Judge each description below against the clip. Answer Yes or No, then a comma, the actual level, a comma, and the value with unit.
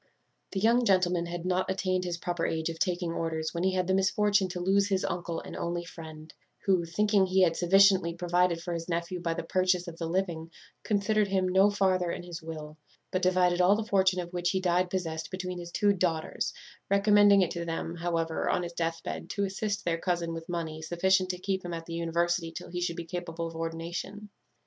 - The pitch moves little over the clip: Yes, narrow, 2.1 semitones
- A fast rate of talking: Yes, fast, 215 wpm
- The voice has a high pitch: No, medium, 175 Hz